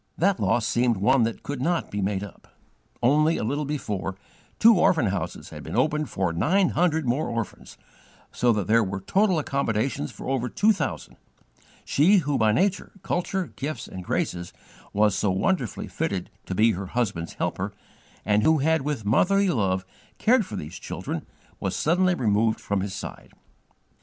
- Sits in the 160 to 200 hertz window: No, low, 120 Hz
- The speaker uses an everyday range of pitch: No, wide, 7.8 semitones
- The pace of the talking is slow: No, average, 170 wpm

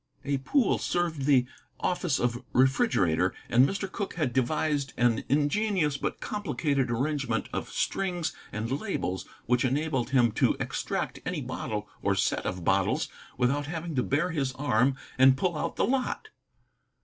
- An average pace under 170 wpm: Yes, average, 150 wpm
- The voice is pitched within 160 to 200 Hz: No, medium, 140 Hz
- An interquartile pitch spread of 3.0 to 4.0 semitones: No, average, 5.0 semitones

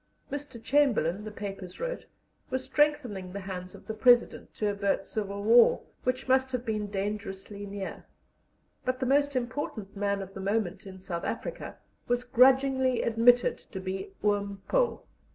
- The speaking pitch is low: No, high, 215 Hz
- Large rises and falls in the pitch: No, average, 4.5 semitones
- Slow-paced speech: No, average, 155 wpm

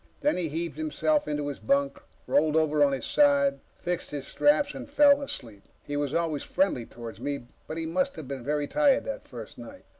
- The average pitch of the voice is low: No, medium, 160 Hz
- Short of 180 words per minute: No, fast, 205 wpm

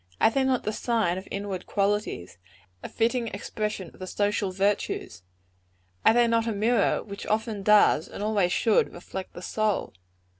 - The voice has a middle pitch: No, high, 210 Hz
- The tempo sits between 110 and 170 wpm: Yes, average, 165 wpm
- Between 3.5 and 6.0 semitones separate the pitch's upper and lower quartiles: No, narrow, 2.6 semitones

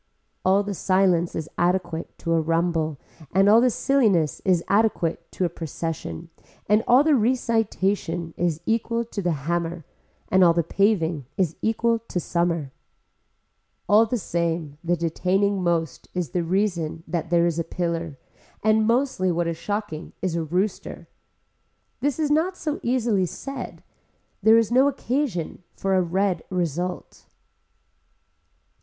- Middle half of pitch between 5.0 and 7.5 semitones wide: No, average, 4.6 semitones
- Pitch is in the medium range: Yes, medium, 180 Hz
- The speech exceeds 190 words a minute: No, average, 145 wpm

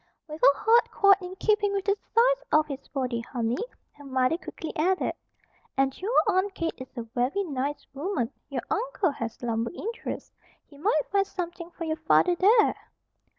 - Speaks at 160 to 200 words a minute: Yes, average, 175 wpm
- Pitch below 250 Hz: No, very high, 330 Hz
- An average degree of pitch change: No, wide, 6.8 semitones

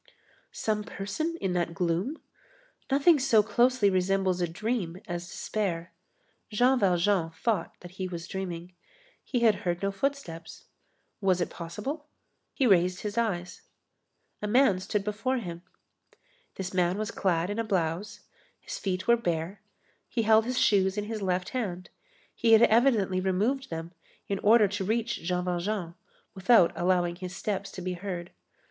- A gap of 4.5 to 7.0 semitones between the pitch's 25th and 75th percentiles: No, average, 3.9 semitones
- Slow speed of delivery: No, average, 155 wpm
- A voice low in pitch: No, high, 195 Hz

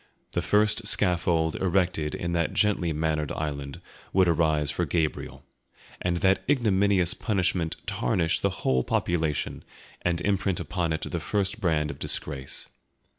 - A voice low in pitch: Yes, very low, 85 Hz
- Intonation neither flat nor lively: Yes, average, 3.6 semitones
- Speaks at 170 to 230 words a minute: No, slow, 135 wpm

